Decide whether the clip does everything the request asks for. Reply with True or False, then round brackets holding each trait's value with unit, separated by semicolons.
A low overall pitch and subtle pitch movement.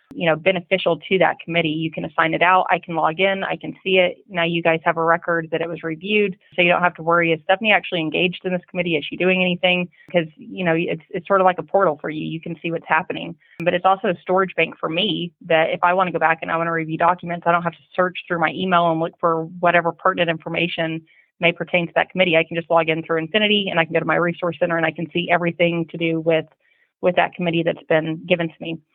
False (170 Hz; 1.7 semitones)